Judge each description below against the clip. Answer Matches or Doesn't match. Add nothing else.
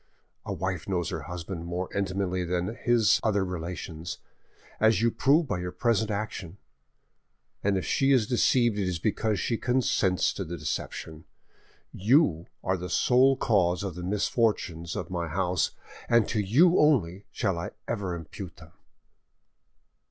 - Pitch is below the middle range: Matches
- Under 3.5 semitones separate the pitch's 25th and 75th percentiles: Doesn't match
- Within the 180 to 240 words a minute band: Doesn't match